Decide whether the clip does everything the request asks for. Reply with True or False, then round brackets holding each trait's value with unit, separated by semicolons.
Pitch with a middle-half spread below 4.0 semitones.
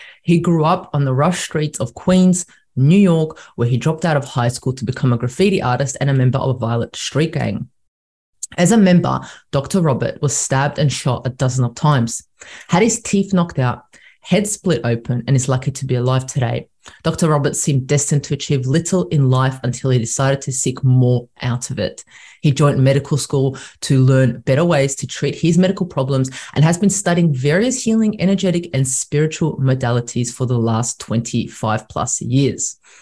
False (4.6 semitones)